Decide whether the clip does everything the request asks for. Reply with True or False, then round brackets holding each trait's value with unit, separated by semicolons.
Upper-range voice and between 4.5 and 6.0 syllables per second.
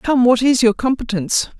True (240 Hz; 5.4 syllables/s)